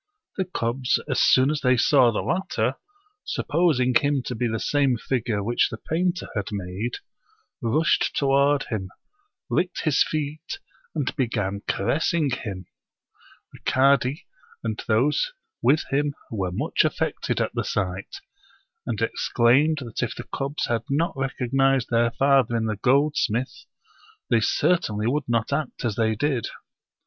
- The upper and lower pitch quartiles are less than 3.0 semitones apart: No, average, 4.3 semitones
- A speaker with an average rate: Yes, average, 145 wpm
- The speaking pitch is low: Yes, low, 130 Hz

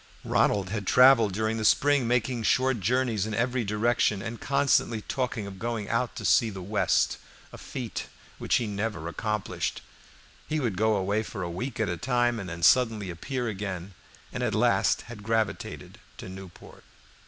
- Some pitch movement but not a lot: Yes, average, 3.4 semitones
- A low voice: Yes, low, 110 Hz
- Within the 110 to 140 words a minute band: No, average, 175 wpm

